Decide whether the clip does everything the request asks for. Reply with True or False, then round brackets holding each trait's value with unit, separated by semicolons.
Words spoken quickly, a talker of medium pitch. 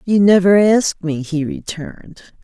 False (150 wpm; 180 Hz)